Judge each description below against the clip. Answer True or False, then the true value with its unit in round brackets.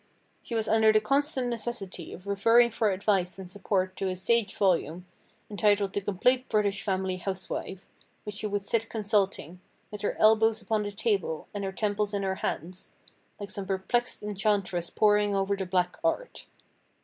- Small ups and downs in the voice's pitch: True (2.3 semitones)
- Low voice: False (205 Hz)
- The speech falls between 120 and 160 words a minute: False (170 wpm)